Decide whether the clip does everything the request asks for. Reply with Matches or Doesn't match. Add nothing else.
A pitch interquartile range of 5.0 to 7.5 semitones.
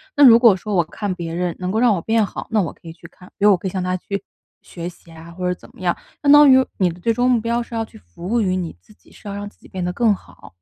Doesn't match